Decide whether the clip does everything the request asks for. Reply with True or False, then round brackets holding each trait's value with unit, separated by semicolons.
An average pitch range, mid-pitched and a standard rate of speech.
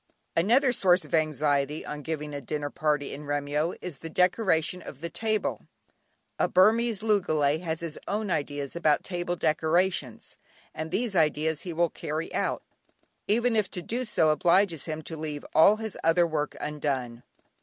True (3.9 semitones; 160 Hz; 165 wpm)